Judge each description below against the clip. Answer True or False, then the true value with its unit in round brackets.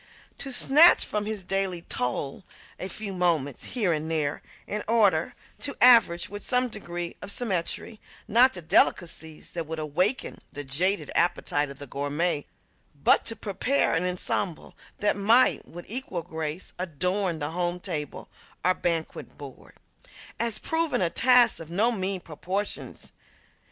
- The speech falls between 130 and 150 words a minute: True (145 wpm)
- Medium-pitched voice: True (180 Hz)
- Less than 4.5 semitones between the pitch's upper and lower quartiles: False (4.8 semitones)